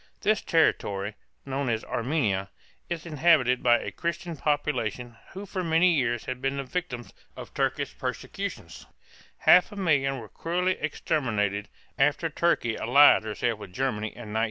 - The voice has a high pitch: No, low, 135 Hz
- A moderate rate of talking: Yes, average, 150 wpm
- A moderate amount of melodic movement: No, wide, 6.1 semitones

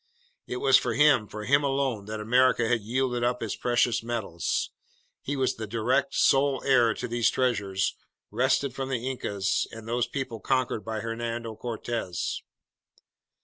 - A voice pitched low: Yes, low, 120 Hz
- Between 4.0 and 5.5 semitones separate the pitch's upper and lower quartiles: No, average, 2.7 semitones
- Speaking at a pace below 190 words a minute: Yes, average, 155 wpm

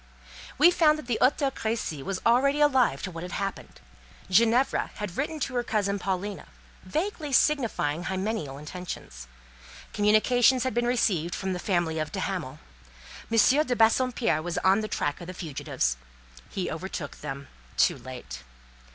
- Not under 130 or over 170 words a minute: Yes, average, 155 wpm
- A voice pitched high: Yes, high, 205 Hz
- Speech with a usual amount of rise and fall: No, wide, 6.5 semitones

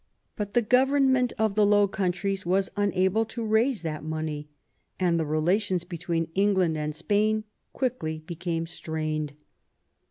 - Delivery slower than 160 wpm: Yes, average, 140 wpm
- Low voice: No, medium, 185 Hz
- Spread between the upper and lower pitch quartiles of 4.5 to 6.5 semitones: Yes, average, 4.8 semitones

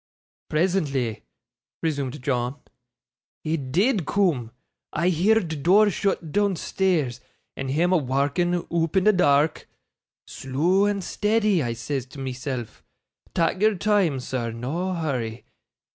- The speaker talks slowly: Yes, slow, 120 wpm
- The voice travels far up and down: Yes, wide, 6.1 semitones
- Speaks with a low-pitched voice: No, medium, 160 Hz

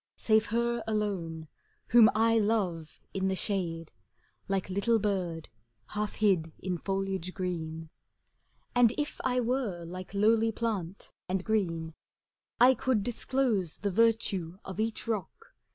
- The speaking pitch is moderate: No, high, 200 Hz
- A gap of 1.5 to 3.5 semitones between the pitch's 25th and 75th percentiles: No, average, 4.1 semitones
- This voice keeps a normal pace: No, slow, 130 wpm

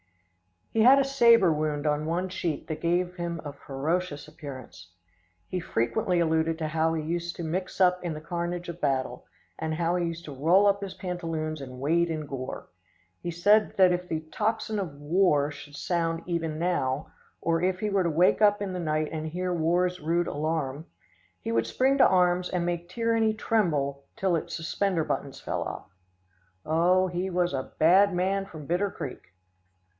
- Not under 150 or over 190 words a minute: Yes, average, 185 wpm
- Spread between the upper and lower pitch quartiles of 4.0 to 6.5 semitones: No, average, 2.9 semitones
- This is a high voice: No, medium, 170 Hz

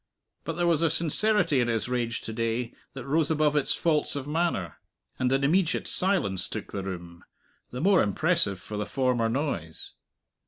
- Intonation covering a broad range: Yes, wide, 6.3 semitones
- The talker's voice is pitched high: No, low, 135 Hz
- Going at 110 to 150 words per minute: No, average, 180 wpm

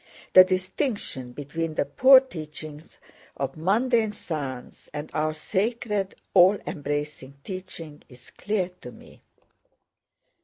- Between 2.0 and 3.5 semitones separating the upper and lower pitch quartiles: No, wide, 5.6 semitones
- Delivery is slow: Yes, slow, 110 wpm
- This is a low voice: No, medium, 165 Hz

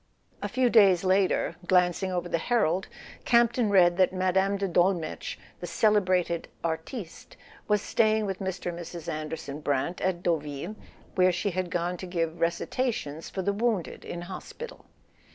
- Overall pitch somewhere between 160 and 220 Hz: Yes, medium, 185 Hz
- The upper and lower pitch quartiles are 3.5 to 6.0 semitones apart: No, average, 2.8 semitones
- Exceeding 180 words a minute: No, average, 155 wpm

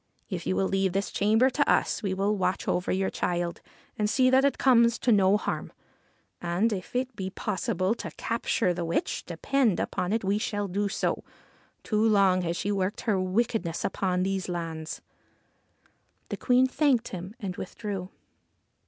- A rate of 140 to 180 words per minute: Yes, average, 170 wpm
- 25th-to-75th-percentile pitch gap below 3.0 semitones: No, average, 3.6 semitones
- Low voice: No, high, 195 Hz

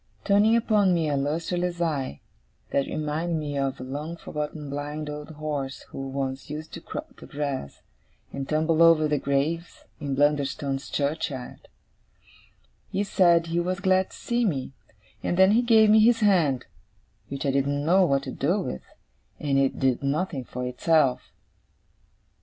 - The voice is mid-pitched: Yes, medium, 150 Hz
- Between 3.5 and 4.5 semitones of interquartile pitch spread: Yes, average, 4.0 semitones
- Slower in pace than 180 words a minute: Yes, average, 160 wpm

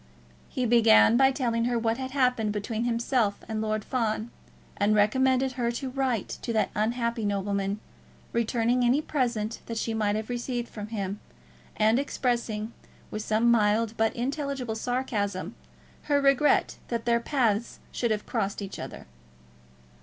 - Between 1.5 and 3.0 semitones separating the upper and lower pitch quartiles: Yes, average, 2.7 semitones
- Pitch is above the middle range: Yes, high, 230 Hz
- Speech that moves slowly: No, average, 150 wpm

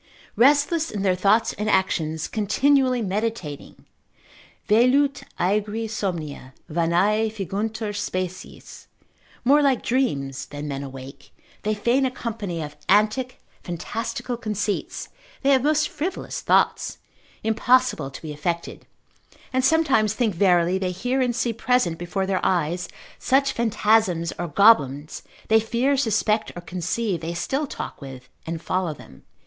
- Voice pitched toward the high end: Yes, high, 210 Hz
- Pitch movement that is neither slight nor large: No, wide, 5.9 semitones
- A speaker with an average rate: No, slow, 130 wpm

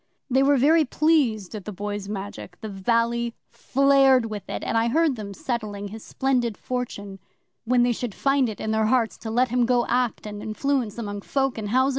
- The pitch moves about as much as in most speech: Yes, average, 3.7 semitones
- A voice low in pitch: No, high, 235 Hz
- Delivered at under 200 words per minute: No, fast, 205 wpm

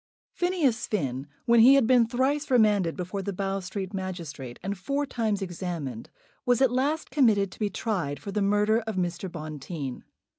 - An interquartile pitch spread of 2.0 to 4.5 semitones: No, average, 5.0 semitones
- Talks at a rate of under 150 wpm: No, average, 175 wpm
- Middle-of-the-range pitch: No, high, 200 Hz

